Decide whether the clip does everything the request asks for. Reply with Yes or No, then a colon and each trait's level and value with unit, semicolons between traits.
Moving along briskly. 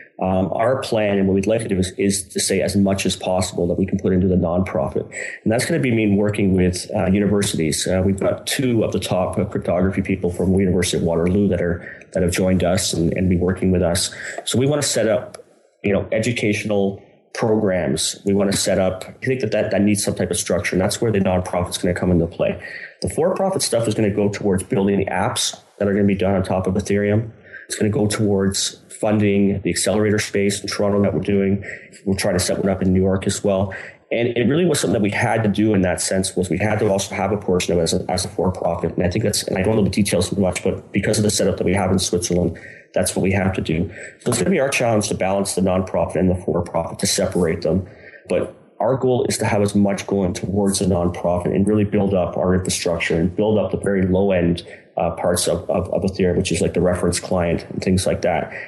Yes: fast, 260 wpm